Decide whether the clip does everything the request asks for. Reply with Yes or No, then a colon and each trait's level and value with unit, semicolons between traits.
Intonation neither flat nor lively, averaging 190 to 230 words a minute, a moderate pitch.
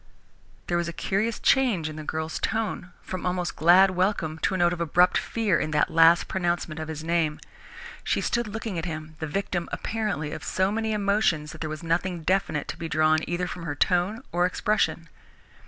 Yes: average, 3.5 semitones; average, 200 wpm; medium, 175 Hz